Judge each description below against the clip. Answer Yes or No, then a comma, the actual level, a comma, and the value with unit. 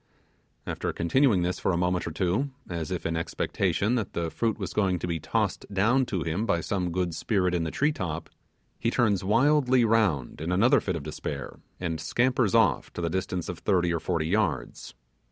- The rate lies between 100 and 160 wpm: No, average, 200 wpm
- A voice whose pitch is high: No, very low, 90 Hz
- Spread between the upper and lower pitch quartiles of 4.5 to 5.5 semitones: Yes, average, 4.8 semitones